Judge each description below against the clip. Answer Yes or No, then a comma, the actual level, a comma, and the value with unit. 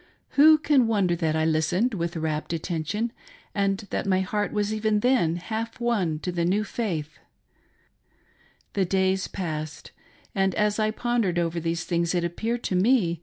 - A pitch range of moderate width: Yes, average, 4.3 semitones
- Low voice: No, high, 190 Hz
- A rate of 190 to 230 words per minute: No, average, 170 wpm